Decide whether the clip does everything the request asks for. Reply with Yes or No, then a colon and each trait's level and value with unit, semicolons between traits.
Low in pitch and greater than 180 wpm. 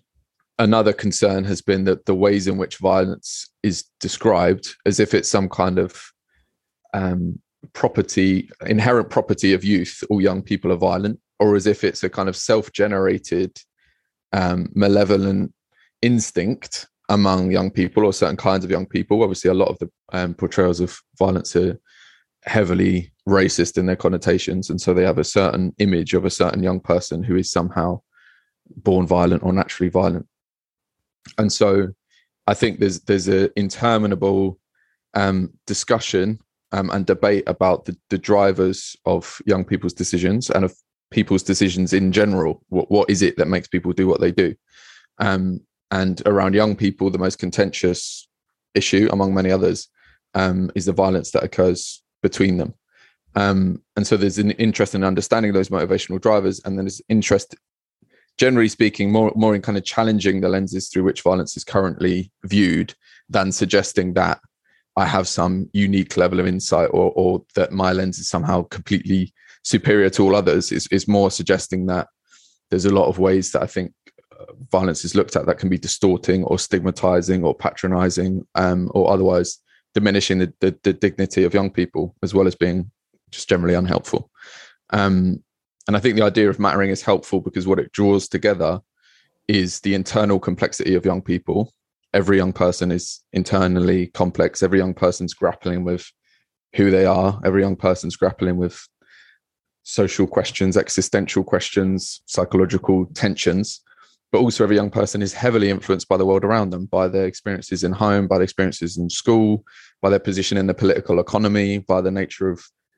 No: very low, 95 Hz; average, 170 wpm